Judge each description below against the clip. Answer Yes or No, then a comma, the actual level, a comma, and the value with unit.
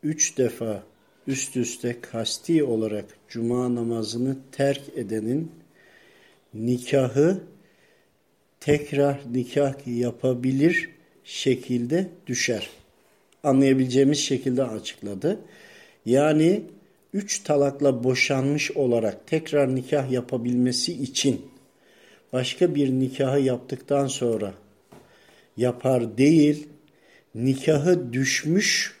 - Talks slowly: Yes, slow, 75 wpm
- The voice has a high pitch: No, low, 130 Hz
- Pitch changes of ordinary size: Yes, average, 3.2 semitones